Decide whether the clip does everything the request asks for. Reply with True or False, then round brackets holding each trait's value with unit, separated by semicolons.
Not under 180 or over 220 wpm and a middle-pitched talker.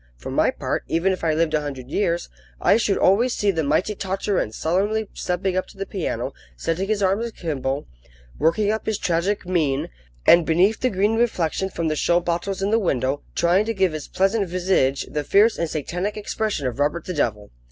True (200 wpm; 180 Hz)